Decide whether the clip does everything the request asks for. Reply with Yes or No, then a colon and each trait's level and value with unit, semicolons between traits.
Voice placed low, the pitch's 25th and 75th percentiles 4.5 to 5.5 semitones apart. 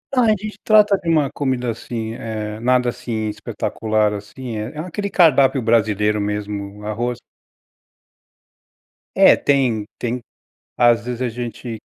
No: low, 120 Hz; average, 3.7 semitones